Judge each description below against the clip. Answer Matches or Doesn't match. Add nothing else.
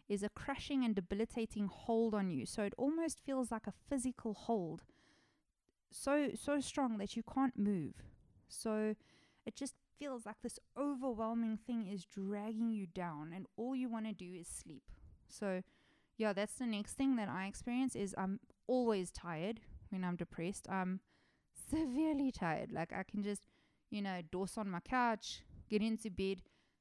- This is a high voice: Matches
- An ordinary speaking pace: Matches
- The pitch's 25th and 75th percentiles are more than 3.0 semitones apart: Matches